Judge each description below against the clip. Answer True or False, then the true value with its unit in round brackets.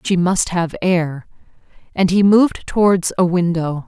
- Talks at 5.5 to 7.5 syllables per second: False (4.4 syllables/s)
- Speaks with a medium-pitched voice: True (180 Hz)